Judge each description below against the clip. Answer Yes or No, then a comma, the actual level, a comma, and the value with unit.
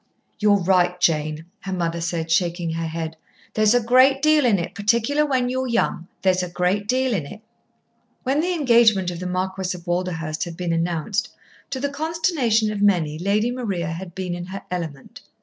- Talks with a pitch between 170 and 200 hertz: Yes, high, 190 Hz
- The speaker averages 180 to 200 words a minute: Yes, average, 185 wpm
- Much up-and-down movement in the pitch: Yes, wide, 5.7 semitones